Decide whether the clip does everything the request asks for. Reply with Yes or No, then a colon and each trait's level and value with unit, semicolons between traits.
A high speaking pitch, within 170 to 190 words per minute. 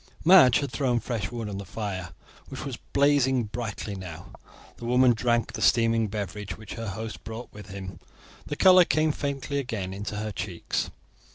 No: low, 115 Hz; average, 175 wpm